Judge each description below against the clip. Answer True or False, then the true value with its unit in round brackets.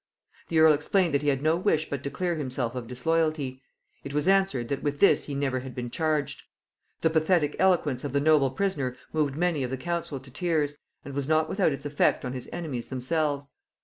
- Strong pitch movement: False (3.3 semitones)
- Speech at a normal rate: False (215 wpm)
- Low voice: False (145 Hz)